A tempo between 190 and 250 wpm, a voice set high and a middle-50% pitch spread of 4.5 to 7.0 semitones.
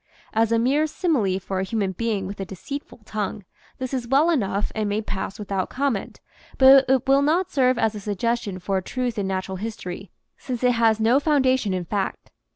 Yes: average, 200 wpm; high, 225 Hz; average, 4.9 semitones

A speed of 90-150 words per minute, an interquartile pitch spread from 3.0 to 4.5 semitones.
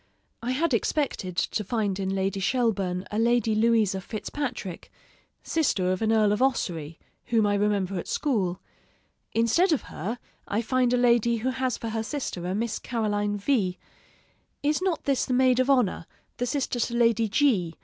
No: average, 170 wpm; average, 4.2 semitones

